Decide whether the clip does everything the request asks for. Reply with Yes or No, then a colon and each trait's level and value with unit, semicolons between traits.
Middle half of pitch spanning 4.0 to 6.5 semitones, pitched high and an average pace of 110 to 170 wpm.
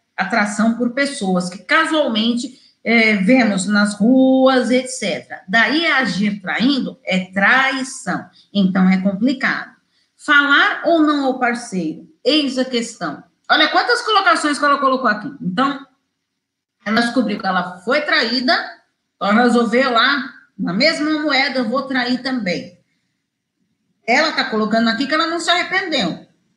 Yes: average, 4.4 semitones; very high, 255 Hz; average, 135 wpm